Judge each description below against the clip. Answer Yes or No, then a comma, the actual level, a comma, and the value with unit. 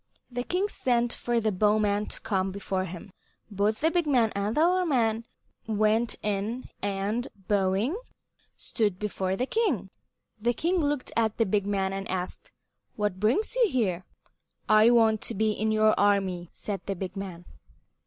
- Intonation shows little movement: No, average, 3.6 semitones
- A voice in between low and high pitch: No, high, 215 Hz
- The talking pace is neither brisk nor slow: Yes, average, 165 wpm